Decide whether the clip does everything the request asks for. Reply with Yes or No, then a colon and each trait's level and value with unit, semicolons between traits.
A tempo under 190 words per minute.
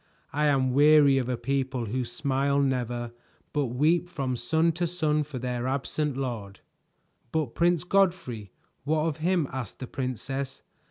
Yes: average, 155 wpm